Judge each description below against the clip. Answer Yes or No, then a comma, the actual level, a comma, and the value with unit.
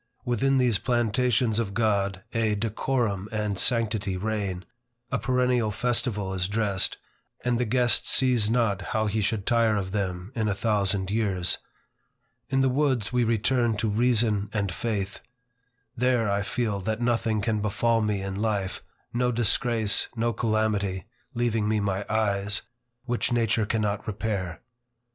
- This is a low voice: Yes, low, 110 Hz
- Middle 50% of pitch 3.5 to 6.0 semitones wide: No, average, 2.8 semitones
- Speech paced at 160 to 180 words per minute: No, average, 145 wpm